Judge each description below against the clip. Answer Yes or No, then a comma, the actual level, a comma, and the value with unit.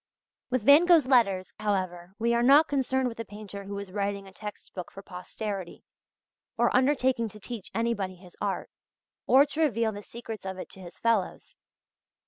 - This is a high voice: Yes, high, 215 Hz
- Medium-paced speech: Yes, average, 180 wpm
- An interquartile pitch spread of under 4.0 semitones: No, average, 4.4 semitones